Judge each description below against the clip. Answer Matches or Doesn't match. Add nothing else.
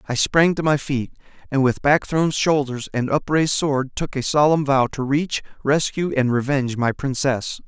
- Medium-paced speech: Matches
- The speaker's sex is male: Matches